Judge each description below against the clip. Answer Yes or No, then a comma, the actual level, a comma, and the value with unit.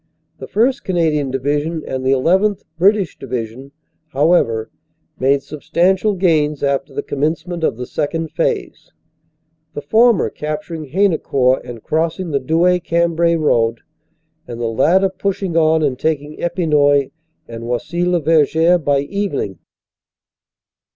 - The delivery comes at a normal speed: No, slow, 130 wpm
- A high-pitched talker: No, medium, 155 Hz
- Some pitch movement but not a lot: Yes, average, 4.2 semitones